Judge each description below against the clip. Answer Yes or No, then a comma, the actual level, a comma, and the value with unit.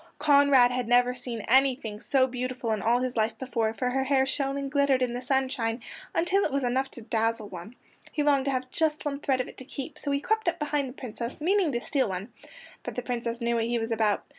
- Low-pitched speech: No, very high, 255 Hz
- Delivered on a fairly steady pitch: No, average, 3.0 semitones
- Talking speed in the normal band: No, fast, 240 wpm